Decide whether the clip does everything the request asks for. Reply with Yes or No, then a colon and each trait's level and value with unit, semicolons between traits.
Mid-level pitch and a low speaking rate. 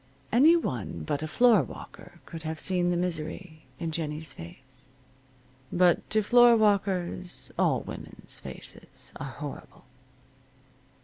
Yes: medium, 170 Hz; slow, 115 wpm